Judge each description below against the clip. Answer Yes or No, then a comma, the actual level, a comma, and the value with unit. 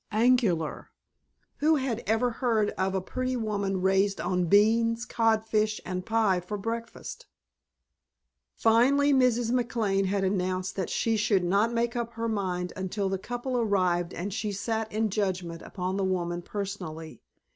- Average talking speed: Yes, average, 145 wpm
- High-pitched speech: Yes, high, 210 Hz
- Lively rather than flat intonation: No, average, 3.6 semitones